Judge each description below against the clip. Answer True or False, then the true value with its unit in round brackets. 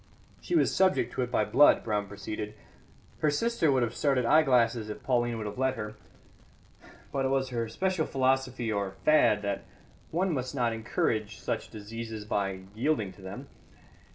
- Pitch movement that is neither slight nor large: True (4.2 semitones)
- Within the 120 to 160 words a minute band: False (170 wpm)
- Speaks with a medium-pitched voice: False (120 Hz)